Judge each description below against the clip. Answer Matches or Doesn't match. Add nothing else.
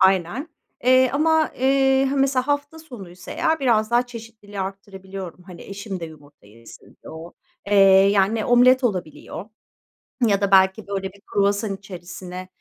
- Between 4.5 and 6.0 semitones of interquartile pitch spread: Matches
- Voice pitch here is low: Doesn't match